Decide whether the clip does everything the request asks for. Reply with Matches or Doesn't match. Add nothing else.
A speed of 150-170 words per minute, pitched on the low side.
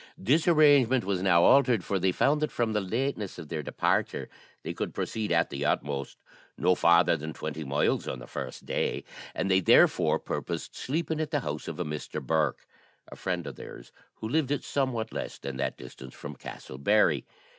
Doesn't match